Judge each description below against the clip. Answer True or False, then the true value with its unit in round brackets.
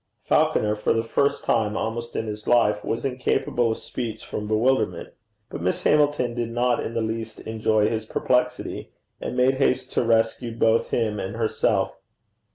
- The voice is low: True (115 Hz)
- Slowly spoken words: False (165 wpm)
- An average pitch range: False (2.1 semitones)